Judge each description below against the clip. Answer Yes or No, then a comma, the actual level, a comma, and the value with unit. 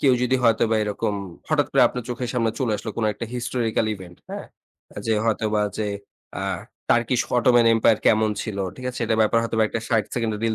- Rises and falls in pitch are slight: Yes, narrow, 1.8 semitones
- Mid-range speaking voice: No, low, 115 Hz